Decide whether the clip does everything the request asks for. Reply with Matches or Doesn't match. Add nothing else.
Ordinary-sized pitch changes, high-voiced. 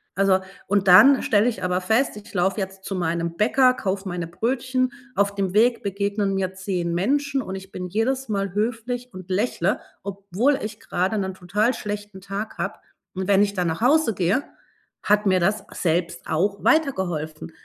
Matches